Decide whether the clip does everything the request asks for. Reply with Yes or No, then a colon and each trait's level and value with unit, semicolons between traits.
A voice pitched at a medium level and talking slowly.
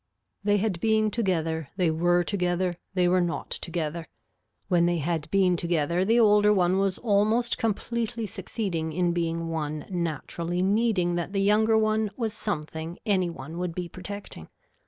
No: medium, 180 Hz; average, 155 wpm